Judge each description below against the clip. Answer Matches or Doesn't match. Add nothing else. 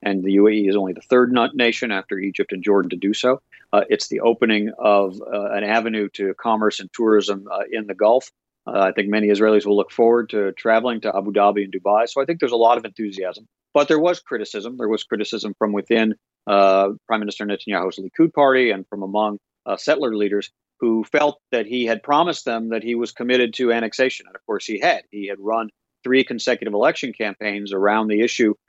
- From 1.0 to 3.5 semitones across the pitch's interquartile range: Matches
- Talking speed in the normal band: Doesn't match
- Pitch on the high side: Doesn't match